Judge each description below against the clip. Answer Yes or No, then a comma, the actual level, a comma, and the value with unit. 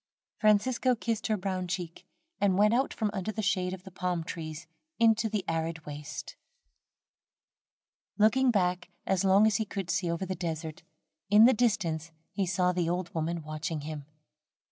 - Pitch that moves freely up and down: No, average, 4.2 semitones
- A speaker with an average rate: Yes, average, 165 wpm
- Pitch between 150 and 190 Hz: Yes, medium, 185 Hz